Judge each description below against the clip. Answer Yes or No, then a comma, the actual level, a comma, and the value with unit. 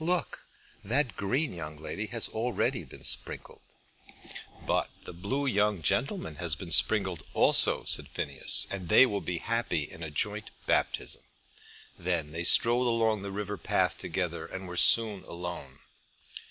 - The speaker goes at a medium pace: Yes, average, 150 wpm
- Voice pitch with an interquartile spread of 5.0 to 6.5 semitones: Yes, average, 5.3 semitones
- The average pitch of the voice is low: Yes, low, 100 Hz